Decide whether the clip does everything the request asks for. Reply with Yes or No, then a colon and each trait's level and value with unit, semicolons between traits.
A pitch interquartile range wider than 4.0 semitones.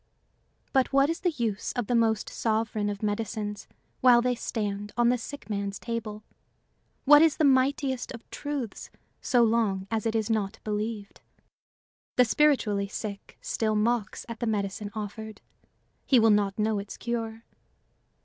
No: average, 2.8 semitones